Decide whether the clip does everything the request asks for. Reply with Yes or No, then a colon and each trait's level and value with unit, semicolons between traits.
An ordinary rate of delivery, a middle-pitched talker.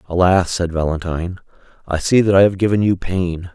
No: average, 185 wpm; very low, 90 Hz